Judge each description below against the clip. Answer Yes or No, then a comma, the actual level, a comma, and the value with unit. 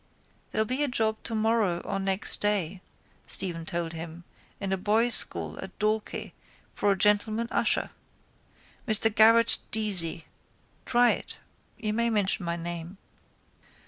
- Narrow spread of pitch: No, average, 4.0 semitones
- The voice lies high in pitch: Yes, high, 205 Hz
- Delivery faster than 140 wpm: No, slow, 135 wpm